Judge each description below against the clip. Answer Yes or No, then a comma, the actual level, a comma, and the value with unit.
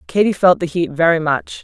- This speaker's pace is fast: Yes, fast, 220 wpm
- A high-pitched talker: No, medium, 170 Hz